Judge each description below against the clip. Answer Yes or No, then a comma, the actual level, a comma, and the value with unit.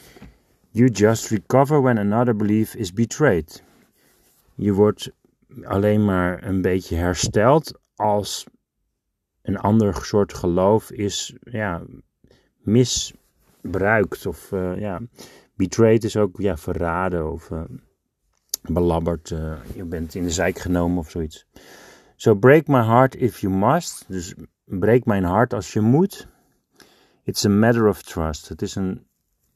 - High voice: No, low, 100 Hz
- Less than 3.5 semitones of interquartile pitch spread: No, average, 4.4 semitones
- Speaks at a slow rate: Yes, slow, 130 wpm